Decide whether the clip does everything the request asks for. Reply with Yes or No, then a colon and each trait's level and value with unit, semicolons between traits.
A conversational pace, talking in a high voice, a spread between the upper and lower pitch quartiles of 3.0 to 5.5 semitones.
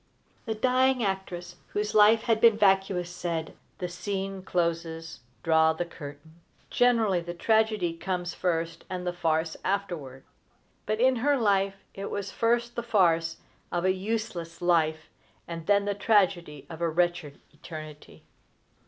No: average, 145 wpm; medium, 180 Hz; average, 3.9 semitones